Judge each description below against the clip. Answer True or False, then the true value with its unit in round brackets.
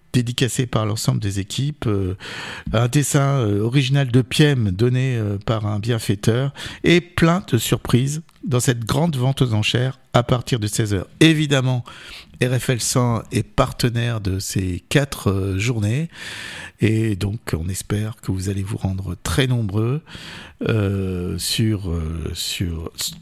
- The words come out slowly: True (130 wpm)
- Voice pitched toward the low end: True (120 Hz)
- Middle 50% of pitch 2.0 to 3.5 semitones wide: False (4.7 semitones)